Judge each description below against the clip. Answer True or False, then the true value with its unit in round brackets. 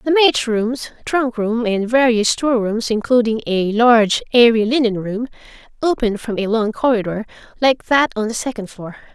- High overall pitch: True (230 Hz)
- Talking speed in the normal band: True (170 wpm)